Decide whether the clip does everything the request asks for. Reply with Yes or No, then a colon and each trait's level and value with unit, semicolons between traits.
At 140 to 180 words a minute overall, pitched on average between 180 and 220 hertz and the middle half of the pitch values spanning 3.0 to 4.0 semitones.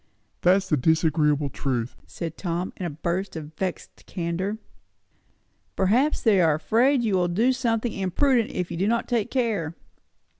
No: average, 155 wpm; medium, 185 Hz; wide, 5.6 semitones